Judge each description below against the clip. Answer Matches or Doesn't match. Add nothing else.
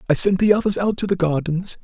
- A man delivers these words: Matches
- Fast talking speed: Matches